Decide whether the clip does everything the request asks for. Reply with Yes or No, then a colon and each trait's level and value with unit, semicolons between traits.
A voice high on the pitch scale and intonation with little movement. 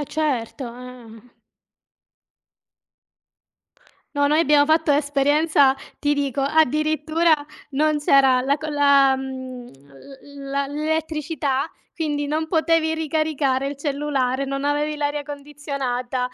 Yes: very high, 285 Hz; narrow, 2.2 semitones